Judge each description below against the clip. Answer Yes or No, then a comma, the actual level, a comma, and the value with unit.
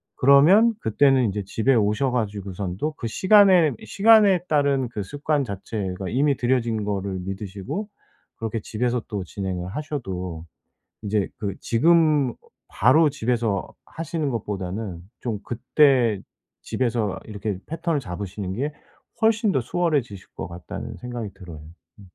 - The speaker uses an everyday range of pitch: No, wide, 6.5 semitones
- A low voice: Yes, low, 115 Hz